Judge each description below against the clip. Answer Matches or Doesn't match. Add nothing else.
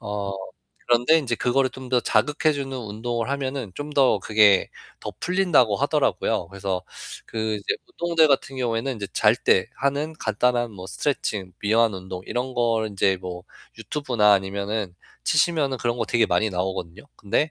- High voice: Doesn't match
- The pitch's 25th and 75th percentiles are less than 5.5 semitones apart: Matches